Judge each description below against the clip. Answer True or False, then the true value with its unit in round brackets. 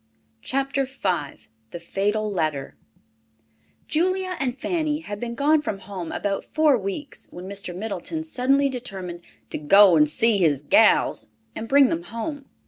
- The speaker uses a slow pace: False (145 wpm)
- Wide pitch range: True (7.4 semitones)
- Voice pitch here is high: True (215 Hz)